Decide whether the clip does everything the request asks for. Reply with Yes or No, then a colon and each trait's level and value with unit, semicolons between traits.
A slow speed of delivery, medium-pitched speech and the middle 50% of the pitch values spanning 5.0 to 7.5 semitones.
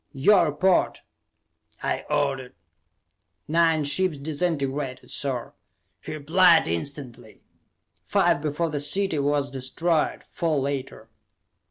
No: slow, 95 wpm; medium, 145 Hz; average, 3.2 semitones